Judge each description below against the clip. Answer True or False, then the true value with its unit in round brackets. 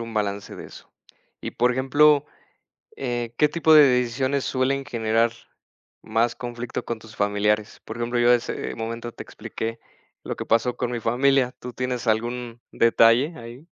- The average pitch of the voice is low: True (120 Hz)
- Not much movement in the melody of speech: True (2.1 semitones)